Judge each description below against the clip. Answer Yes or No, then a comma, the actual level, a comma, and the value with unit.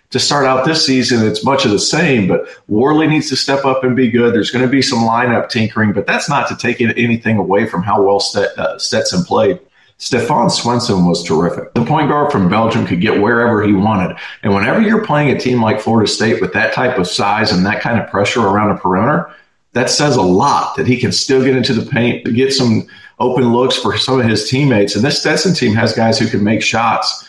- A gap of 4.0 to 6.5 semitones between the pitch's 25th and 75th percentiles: No, average, 3.1 semitones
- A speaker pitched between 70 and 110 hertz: No, low, 120 Hz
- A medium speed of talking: No, fast, 235 wpm